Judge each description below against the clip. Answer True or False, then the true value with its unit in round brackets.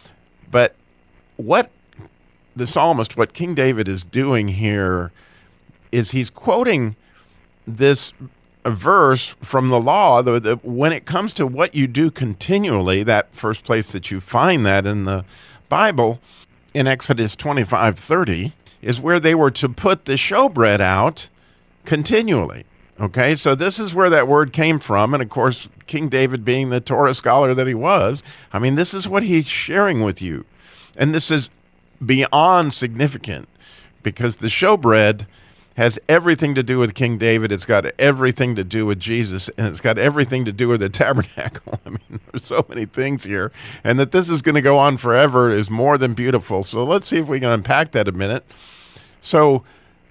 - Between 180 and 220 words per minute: False (170 wpm)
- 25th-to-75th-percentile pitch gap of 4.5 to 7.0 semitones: True (5.0 semitones)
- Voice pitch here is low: True (125 Hz)